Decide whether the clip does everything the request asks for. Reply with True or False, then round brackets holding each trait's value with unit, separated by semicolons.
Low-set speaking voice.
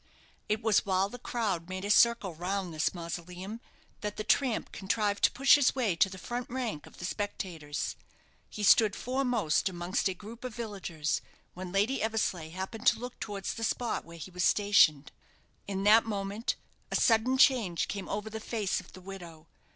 False (205 Hz)